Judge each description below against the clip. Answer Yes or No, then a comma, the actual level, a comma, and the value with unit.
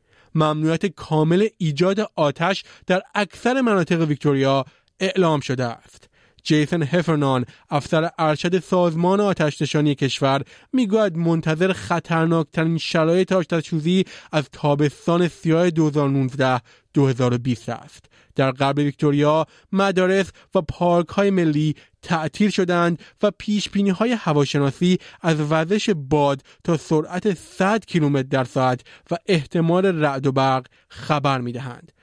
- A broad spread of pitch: No, average, 4.3 semitones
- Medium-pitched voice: Yes, medium, 160 Hz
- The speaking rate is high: No, average, 110 wpm